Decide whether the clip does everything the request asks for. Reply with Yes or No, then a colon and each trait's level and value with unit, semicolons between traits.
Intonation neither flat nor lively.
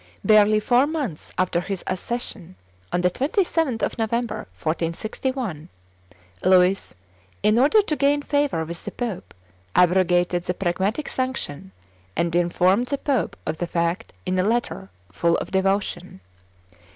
No: wide, 5.9 semitones